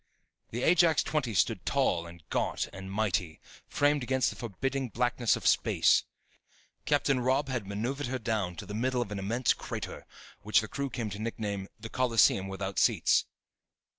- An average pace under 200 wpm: Yes, average, 165 wpm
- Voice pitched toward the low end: Yes, low, 115 Hz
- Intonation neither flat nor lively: Yes, average, 4.5 semitones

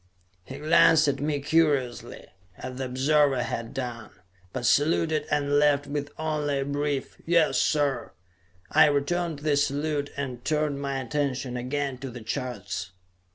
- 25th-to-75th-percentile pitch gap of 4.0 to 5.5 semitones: No, narrow, 2.4 semitones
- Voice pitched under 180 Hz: Yes, medium, 140 Hz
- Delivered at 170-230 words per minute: No, average, 145 wpm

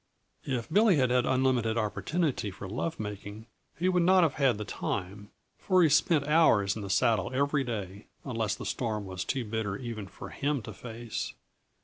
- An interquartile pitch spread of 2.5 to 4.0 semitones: No, wide, 5.5 semitones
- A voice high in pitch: No, low, 120 Hz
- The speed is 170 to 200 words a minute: Yes, average, 175 wpm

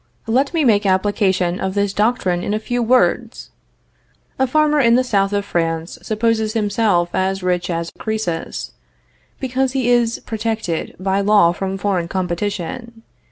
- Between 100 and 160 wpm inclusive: Yes, average, 150 wpm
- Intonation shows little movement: No, average, 3.9 semitones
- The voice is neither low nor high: No, high, 205 Hz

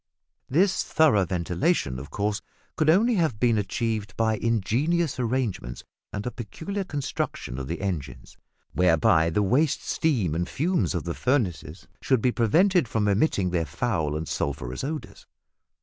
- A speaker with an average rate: Yes, average, 150 wpm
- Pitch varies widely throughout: Yes, wide, 8.7 semitones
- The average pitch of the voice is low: Yes, low, 110 Hz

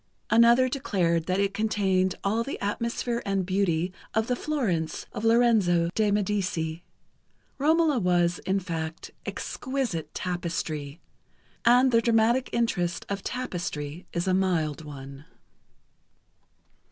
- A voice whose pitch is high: Yes, high, 195 Hz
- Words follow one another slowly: Yes, slow, 115 wpm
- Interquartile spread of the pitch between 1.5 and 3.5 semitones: No, average, 5.3 semitones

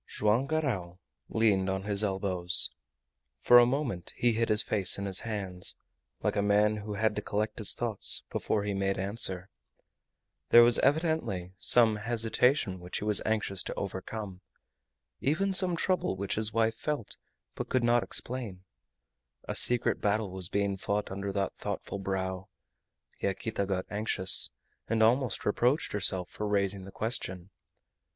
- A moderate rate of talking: Yes, average, 155 wpm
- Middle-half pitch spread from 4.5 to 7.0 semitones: No, average, 3.2 semitones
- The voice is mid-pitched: No, low, 105 Hz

